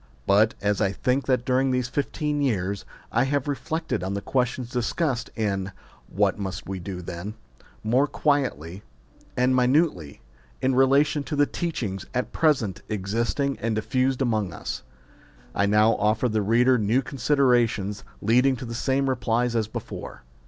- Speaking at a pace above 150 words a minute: Yes, average, 160 wpm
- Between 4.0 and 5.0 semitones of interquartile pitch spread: Yes, average, 4.5 semitones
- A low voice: Yes, low, 120 Hz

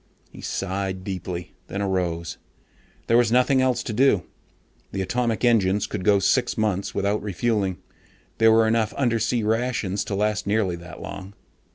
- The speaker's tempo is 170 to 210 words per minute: No, average, 155 wpm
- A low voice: Yes, low, 105 Hz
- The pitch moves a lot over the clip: No, average, 3.2 semitones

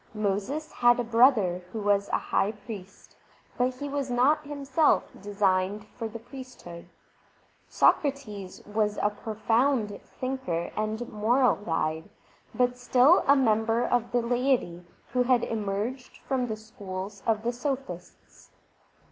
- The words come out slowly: Yes, slow, 130 wpm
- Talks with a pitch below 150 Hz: No, high, 225 Hz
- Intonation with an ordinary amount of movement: Yes, average, 3.8 semitones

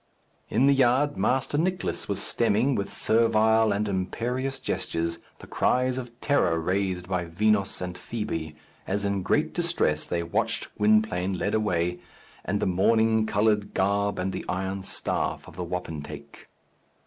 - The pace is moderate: Yes, average, 150 wpm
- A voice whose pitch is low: Yes, low, 100 Hz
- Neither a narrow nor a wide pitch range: Yes, average, 4.3 semitones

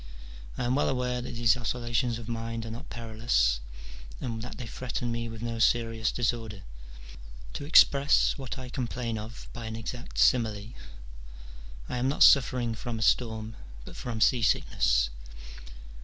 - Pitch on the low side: Yes, low, 115 Hz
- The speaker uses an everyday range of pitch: No, narrow, 1.8 semitones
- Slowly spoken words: No, average, 155 wpm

